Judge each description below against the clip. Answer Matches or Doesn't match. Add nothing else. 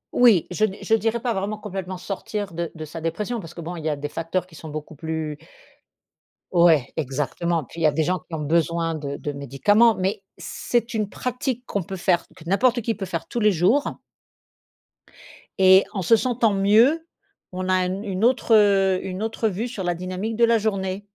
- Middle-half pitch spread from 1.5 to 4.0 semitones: Doesn't match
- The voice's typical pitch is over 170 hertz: Matches